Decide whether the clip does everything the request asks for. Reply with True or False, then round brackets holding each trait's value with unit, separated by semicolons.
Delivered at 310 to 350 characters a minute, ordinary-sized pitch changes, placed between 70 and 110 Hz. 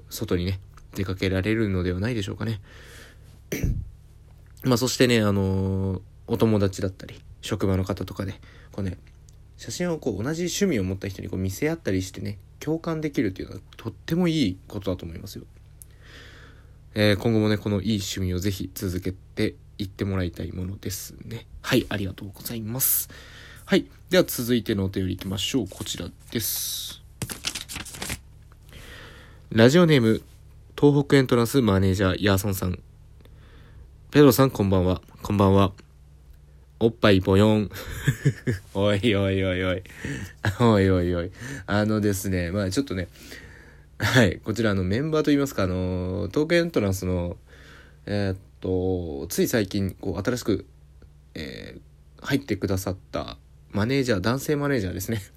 True (330 characters per minute; 3.7 semitones; 100 Hz)